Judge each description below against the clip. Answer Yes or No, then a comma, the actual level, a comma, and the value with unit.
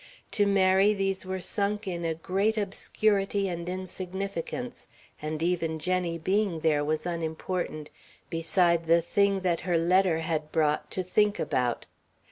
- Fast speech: No, average, 140 wpm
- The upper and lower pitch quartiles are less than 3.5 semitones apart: Yes, average, 3.0 semitones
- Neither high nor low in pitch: Yes, medium, 180 Hz